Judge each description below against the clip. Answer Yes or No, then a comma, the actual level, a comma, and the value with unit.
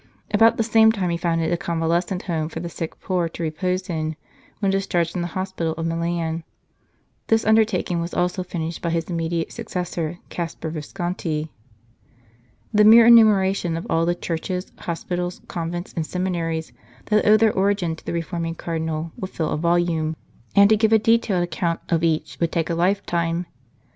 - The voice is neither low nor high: Yes, medium, 175 Hz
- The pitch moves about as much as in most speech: No, narrow, 2.3 semitones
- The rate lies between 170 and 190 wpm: Yes, average, 180 wpm